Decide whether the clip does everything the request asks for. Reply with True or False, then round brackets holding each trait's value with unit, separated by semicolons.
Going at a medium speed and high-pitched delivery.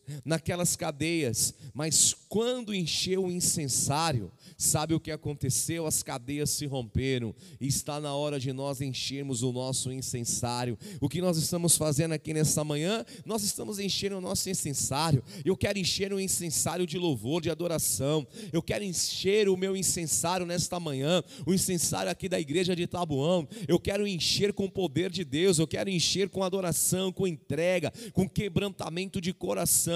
False (165 wpm; 165 Hz)